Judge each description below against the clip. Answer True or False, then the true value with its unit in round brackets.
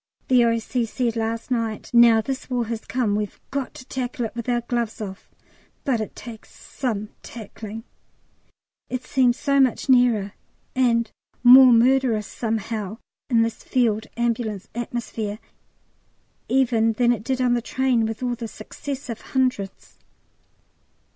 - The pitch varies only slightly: True (2.3 semitones)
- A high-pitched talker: True (235 Hz)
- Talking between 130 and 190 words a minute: True (140 wpm)